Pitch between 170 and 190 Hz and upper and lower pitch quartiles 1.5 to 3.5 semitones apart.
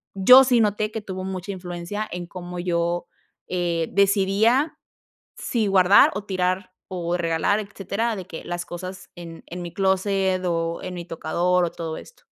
Yes: medium, 185 Hz; narrow, 2.4 semitones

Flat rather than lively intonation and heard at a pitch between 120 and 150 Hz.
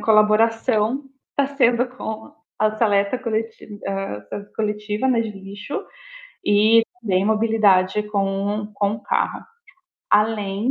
No: narrow, 2.0 semitones; high, 215 Hz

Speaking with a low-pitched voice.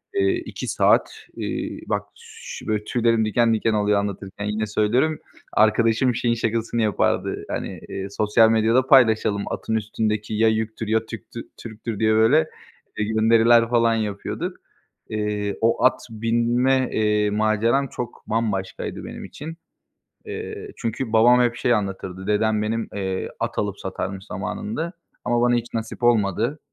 Yes: low, 110 Hz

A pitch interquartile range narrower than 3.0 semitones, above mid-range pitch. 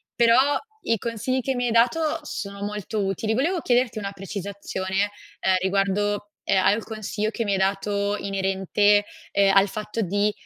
Yes: narrow, 2.6 semitones; high, 205 Hz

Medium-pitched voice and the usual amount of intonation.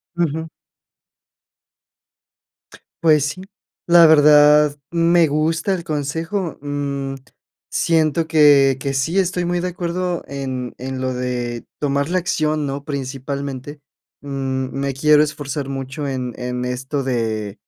Yes: medium, 145 Hz; average, 3.3 semitones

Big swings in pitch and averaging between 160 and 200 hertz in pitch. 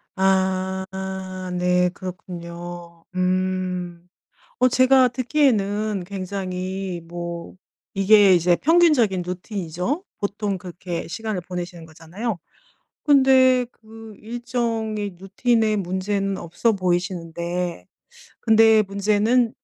No: average, 3.8 semitones; high, 190 Hz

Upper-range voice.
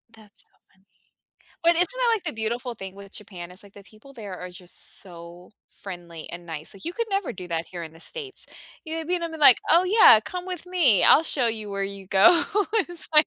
Yes: high, 215 Hz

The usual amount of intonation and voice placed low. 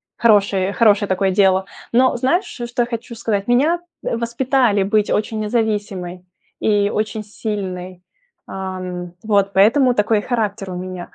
No: average, 3.4 semitones; high, 210 Hz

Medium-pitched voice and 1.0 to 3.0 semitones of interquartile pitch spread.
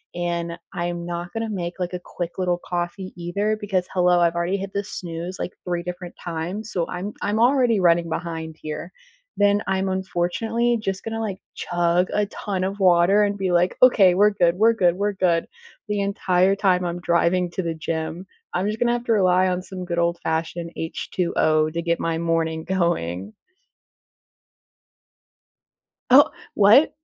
Yes: medium, 180 Hz; narrow, 2.6 semitones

